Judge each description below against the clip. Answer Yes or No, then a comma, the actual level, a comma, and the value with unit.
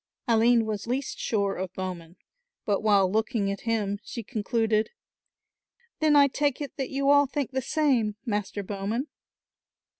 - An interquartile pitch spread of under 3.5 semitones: No, average, 4.7 semitones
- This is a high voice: Yes, high, 225 Hz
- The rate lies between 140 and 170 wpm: Yes, average, 150 wpm